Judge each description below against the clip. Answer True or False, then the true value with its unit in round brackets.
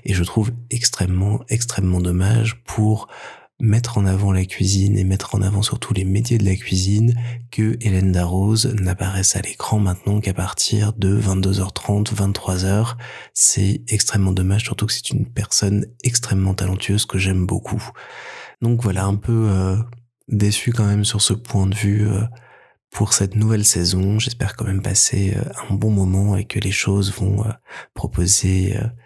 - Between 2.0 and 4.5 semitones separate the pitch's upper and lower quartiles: True (2.6 semitones)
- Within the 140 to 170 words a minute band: True (165 wpm)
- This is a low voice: True (105 Hz)